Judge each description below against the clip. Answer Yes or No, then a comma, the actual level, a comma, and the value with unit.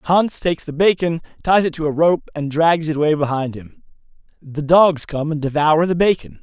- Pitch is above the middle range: No, medium, 155 Hz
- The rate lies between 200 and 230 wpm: Yes, fast, 205 wpm